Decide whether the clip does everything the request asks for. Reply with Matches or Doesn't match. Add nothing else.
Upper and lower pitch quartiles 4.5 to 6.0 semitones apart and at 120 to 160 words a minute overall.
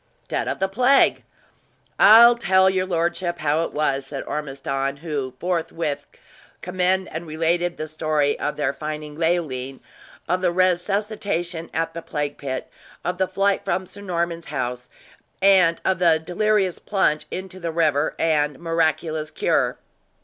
Doesn't match